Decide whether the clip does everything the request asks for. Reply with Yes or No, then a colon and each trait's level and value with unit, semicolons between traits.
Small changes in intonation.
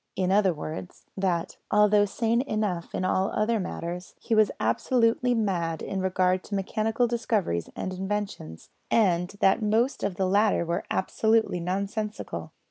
No: average, 3.2 semitones